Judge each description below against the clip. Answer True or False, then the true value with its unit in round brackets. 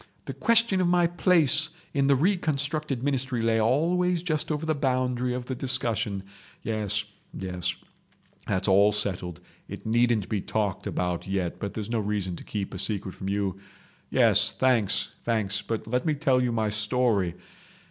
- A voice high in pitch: False (115 Hz)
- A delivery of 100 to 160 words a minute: True (155 wpm)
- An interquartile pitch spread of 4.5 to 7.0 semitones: True (5.6 semitones)